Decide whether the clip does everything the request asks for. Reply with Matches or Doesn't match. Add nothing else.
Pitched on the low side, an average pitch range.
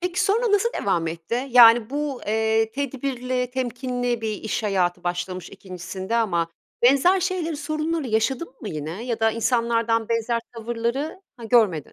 Doesn't match